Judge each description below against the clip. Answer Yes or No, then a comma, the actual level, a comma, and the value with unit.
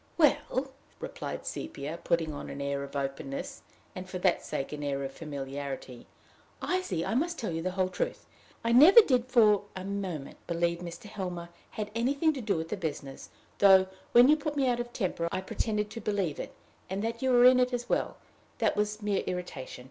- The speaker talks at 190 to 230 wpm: Yes, average, 200 wpm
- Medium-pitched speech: No, high, 195 Hz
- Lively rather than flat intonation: Yes, wide, 6.8 semitones